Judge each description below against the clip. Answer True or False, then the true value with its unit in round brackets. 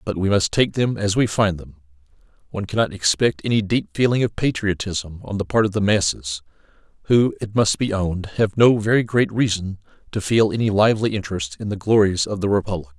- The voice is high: False (100 Hz)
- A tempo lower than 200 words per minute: False (205 wpm)